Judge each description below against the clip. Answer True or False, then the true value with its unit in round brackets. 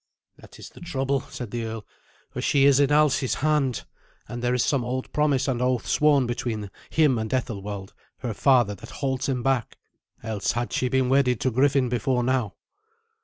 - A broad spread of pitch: False (2.4 semitones)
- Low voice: True (125 Hz)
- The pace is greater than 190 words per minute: False (185 wpm)